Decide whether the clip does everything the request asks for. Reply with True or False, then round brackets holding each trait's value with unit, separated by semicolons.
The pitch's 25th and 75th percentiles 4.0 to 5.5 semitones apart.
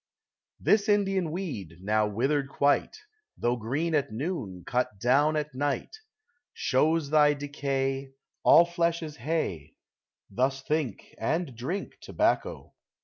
True (4.6 semitones)